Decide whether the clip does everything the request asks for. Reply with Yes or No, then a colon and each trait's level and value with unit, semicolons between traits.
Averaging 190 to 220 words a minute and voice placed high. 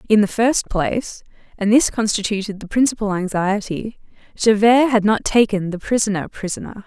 No: average, 150 wpm; high, 210 Hz